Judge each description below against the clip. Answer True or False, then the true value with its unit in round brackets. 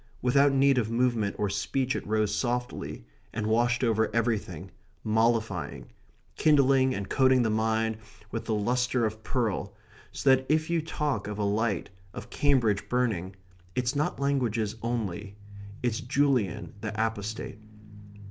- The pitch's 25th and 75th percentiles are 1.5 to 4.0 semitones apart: True (3.3 semitones)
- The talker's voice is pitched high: False (115 Hz)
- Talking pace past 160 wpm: False (140 wpm)